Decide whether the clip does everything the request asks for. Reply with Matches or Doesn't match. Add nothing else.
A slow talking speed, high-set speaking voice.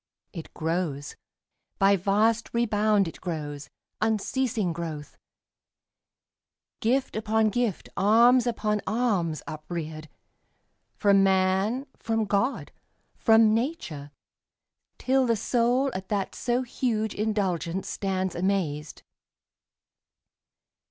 Matches